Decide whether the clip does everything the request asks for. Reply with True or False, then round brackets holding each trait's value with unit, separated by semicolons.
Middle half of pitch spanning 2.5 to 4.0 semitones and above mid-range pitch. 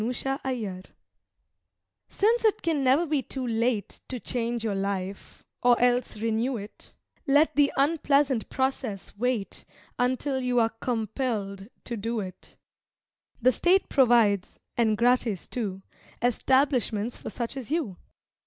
True (3.7 semitones; 245 Hz)